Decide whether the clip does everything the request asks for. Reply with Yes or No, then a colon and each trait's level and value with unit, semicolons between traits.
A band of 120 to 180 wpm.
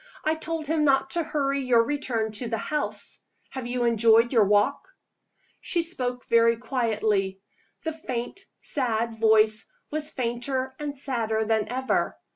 Yes: average, 145 wpm